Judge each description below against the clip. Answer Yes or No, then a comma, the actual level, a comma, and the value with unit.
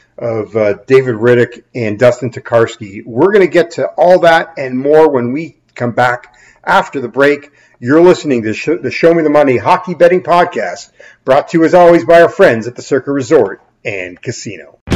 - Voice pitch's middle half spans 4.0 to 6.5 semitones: Yes, wide, 5.5 semitones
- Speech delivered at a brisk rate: No, average, 195 wpm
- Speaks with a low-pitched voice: Yes, low, 130 Hz